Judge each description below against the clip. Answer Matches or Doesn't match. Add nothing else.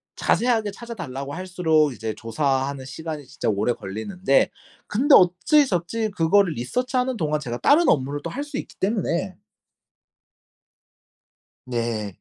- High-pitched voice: Doesn't match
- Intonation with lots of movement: Matches